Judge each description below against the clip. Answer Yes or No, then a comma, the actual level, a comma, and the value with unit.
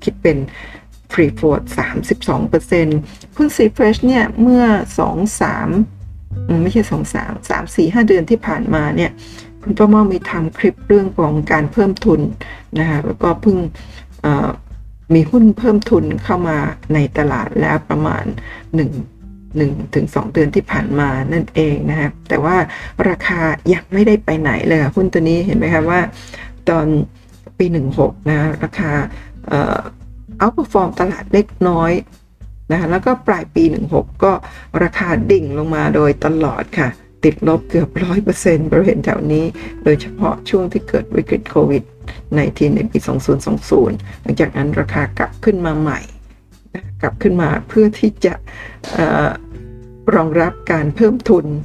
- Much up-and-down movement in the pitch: Yes, wide, 6.1 semitones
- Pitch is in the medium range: Yes, medium, 160 Hz